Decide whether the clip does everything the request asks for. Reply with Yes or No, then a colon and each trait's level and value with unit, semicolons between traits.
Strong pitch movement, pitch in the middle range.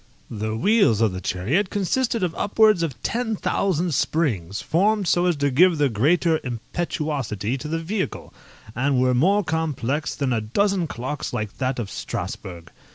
Yes: wide, 7.5 semitones; medium, 150 Hz